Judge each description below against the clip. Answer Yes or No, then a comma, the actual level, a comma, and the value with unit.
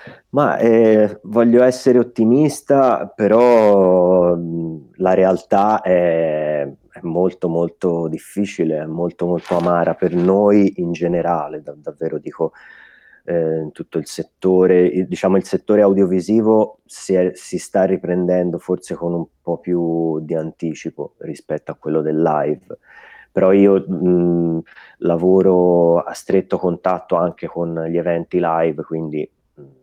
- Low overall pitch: Yes, very low, 90 Hz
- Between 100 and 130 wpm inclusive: Yes, average, 125 wpm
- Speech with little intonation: Yes, narrow, 2.2 semitones